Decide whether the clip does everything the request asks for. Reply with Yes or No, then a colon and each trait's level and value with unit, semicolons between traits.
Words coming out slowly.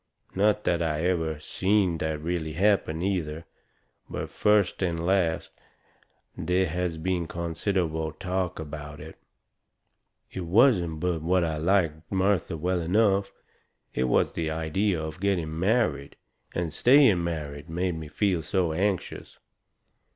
Yes: slow, 130 wpm